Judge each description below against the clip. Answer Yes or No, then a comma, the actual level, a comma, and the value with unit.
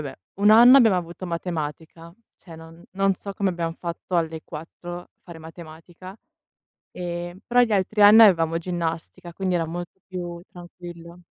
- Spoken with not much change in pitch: Yes, narrow, 2.2 semitones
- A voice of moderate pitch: Yes, medium, 175 Hz